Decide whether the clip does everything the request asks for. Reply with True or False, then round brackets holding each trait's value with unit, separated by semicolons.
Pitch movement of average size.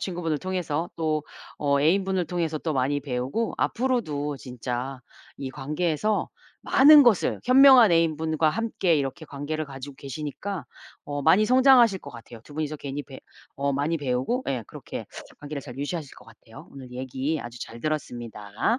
True (5.0 semitones)